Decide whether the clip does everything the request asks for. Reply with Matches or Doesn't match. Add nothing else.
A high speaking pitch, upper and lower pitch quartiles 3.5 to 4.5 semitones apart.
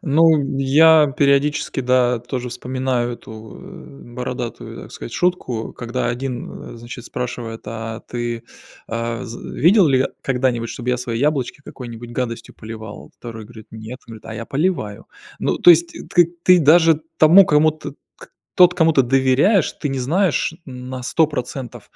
Doesn't match